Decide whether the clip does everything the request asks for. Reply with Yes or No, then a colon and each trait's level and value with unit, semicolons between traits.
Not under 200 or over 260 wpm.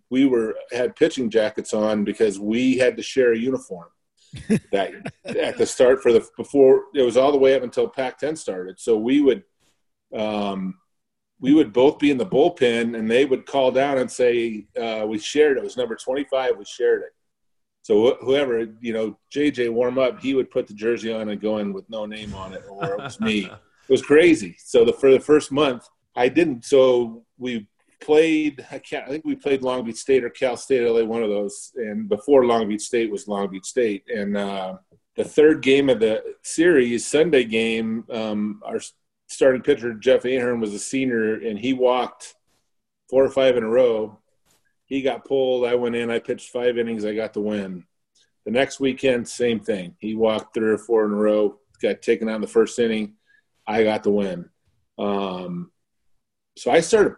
Yes: fast, 205 wpm